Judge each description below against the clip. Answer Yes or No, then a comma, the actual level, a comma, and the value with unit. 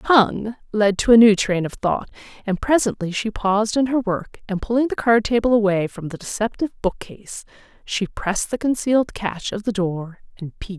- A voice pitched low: No, high, 210 Hz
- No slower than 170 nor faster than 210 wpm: Yes, fast, 205 wpm